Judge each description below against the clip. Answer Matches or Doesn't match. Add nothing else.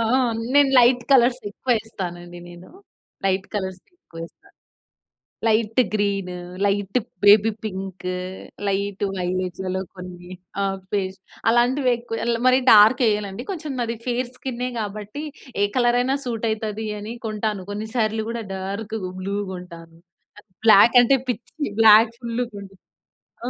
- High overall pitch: Matches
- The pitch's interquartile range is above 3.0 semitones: Matches